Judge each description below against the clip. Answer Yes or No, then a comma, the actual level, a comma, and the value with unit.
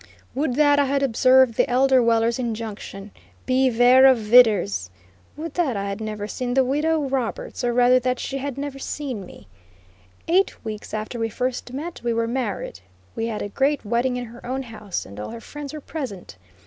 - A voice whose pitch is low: No, very high, 250 Hz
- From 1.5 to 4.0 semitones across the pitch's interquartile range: Yes, average, 3.2 semitones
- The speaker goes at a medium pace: Yes, average, 190 wpm